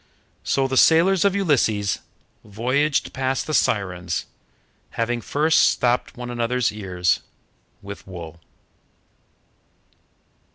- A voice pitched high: No, low, 120 Hz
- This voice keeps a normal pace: No, slow, 95 wpm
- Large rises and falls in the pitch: Yes, wide, 6.0 semitones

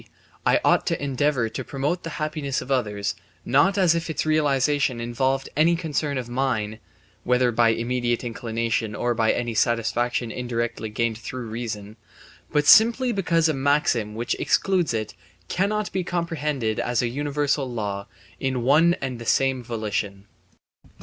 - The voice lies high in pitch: No, low, 130 Hz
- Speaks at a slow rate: No, average, 150 wpm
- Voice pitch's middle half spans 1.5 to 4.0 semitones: No, average, 4.5 semitones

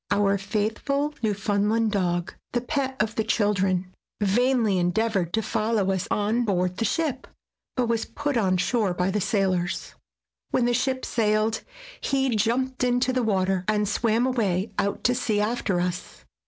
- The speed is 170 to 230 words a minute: No, average, 155 wpm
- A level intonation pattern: No, average, 3.9 semitones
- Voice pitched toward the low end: No, high, 215 Hz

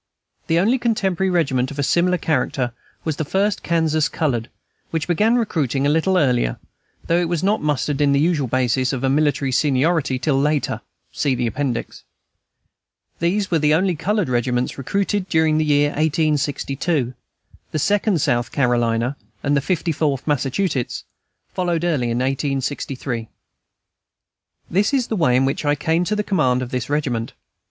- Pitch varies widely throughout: No, average, 4.8 semitones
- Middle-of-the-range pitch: Yes, medium, 150 Hz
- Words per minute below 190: Yes, average, 160 wpm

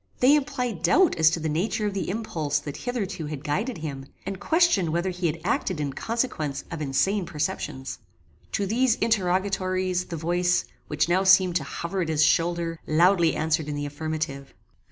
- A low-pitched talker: No, medium, 175 Hz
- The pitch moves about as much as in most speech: Yes, average, 4.1 semitones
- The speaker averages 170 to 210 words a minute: Yes, average, 175 wpm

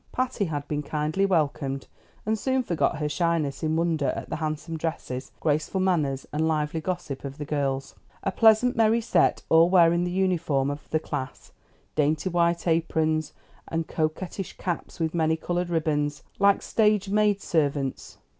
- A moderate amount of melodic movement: Yes, average, 3.6 semitones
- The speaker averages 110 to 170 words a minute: Yes, average, 160 wpm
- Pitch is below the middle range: No, medium, 160 Hz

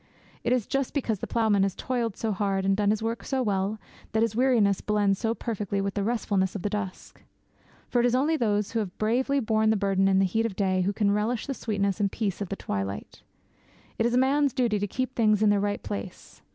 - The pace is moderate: No, fast, 240 wpm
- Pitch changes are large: No, average, 3.1 semitones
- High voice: Yes, high, 210 Hz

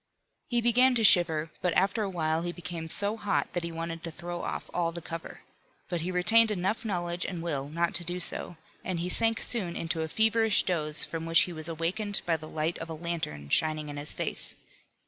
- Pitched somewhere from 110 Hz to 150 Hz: No, medium, 175 Hz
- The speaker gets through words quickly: Yes, fast, 220 wpm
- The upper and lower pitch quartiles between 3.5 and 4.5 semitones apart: No, average, 3.1 semitones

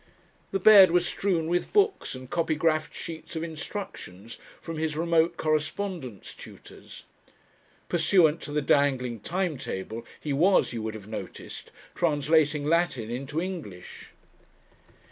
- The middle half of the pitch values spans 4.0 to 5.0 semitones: Yes, average, 4.4 semitones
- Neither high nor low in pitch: Yes, medium, 155 Hz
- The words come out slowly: Yes, slow, 125 wpm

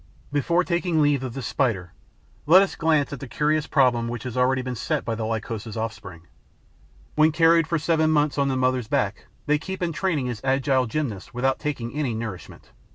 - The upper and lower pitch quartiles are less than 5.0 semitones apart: Yes, average, 4.6 semitones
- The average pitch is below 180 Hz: Yes, low, 135 Hz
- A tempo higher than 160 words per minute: Yes, average, 195 wpm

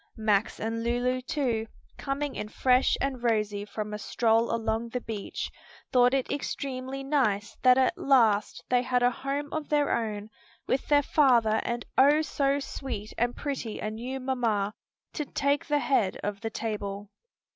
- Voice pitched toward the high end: Yes, high, 245 Hz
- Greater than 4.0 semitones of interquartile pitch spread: No, average, 3.7 semitones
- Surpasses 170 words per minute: No, average, 160 wpm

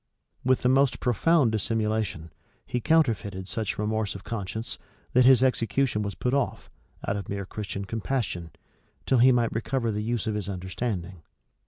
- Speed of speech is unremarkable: Yes, average, 160 wpm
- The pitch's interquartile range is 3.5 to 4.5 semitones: Yes, average, 3.8 semitones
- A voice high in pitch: No, low, 110 Hz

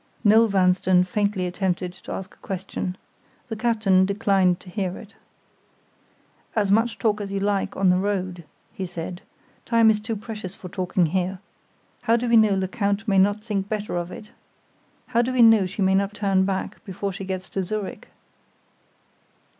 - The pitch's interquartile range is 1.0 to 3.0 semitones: Yes, narrow, 2.4 semitones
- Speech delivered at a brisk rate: No, average, 175 wpm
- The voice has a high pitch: Yes, high, 195 Hz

